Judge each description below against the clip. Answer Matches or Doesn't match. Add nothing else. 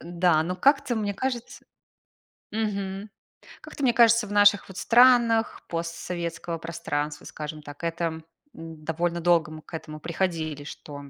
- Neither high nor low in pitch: Matches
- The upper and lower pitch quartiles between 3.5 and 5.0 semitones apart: Matches